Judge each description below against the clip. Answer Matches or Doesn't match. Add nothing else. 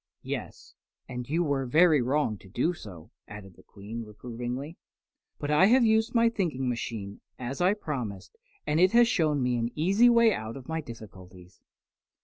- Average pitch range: Doesn't match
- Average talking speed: Matches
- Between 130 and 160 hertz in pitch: Matches